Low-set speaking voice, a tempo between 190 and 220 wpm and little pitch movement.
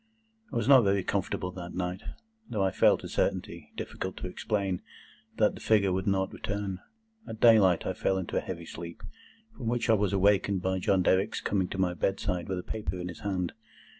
Yes: very low, 95 Hz; average, 200 wpm; narrow, 2.0 semitones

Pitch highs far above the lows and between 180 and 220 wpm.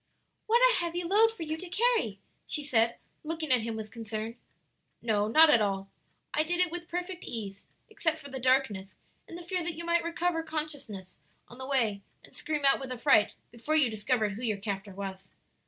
Yes: wide, 7.6 semitones; average, 200 wpm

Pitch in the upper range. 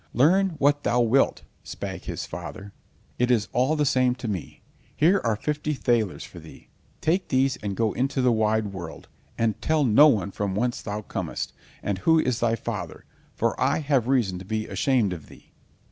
No: low, 120 Hz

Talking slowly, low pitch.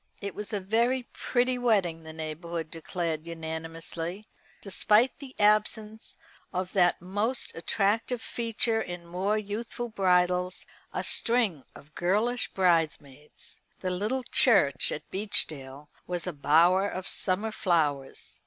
No: slow, 125 wpm; medium, 185 Hz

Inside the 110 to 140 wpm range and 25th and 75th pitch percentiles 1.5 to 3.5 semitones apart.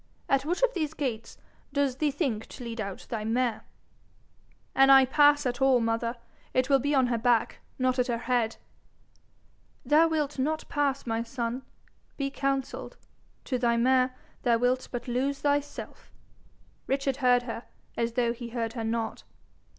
No: average, 165 wpm; average, 2.8 semitones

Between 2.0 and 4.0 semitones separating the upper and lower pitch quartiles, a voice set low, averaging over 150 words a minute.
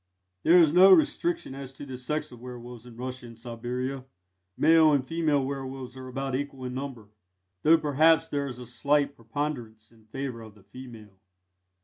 Yes: average, 3.0 semitones; low, 130 Hz; average, 175 wpm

